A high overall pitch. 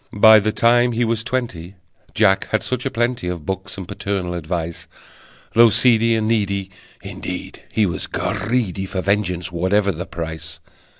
No: low, 100 Hz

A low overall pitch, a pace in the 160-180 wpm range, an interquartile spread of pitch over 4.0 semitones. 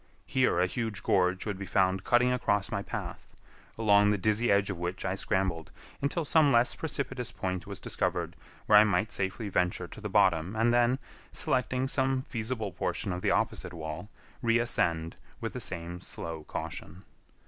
Yes: low, 100 Hz; average, 170 wpm; average, 4.5 semitones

